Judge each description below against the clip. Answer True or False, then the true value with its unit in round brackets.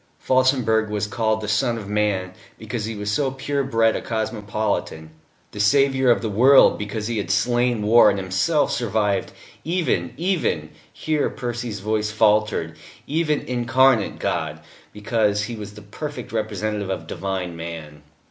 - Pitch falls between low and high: False (110 Hz)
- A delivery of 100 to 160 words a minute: True (150 wpm)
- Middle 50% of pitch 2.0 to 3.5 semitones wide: True (3.1 semitones)